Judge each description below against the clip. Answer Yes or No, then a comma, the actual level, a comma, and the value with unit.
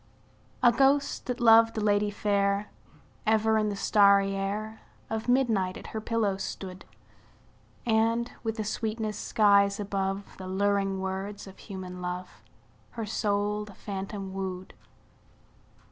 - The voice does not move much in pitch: Yes, narrow, 2.1 semitones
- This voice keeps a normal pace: No, slow, 130 wpm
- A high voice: Yes, high, 205 Hz